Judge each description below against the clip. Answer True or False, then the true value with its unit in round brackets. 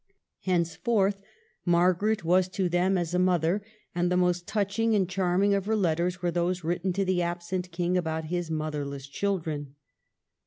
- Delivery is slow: False (160 wpm)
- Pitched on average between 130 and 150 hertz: False (180 Hz)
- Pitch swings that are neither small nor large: False (1.9 semitones)